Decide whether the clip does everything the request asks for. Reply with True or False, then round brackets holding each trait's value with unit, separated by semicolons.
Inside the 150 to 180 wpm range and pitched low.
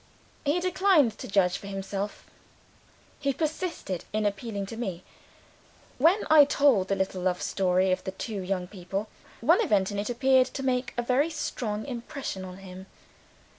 False (165 wpm; 210 Hz)